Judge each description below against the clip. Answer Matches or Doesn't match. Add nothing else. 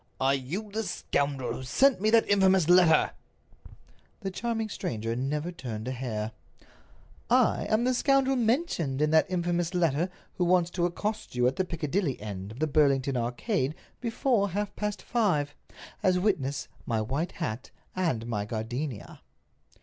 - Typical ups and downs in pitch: Doesn't match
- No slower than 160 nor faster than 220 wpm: Doesn't match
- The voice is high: Doesn't match